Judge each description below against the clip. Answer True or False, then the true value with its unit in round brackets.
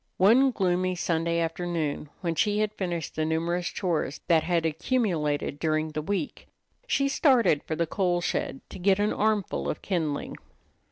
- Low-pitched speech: False (175 Hz)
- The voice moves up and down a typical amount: True (3.9 semitones)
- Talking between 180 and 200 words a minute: False (160 wpm)